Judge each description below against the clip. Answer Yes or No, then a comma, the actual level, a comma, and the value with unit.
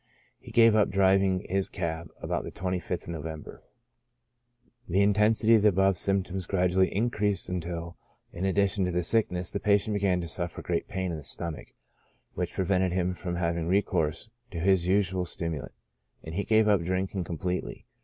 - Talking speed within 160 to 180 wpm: Yes, average, 170 wpm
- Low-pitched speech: Yes, very low, 95 Hz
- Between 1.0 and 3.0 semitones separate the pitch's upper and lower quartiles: Yes, narrow, 2.4 semitones